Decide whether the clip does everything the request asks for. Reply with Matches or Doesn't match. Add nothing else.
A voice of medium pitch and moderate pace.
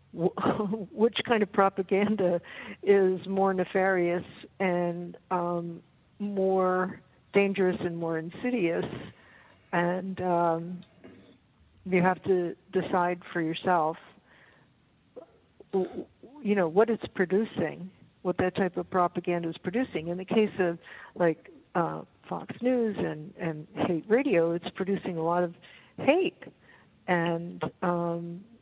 Doesn't match